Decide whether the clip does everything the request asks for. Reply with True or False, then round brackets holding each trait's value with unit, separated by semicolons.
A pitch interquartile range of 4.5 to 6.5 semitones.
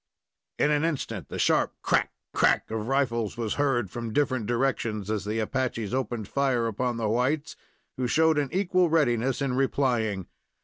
False (3.8 semitones)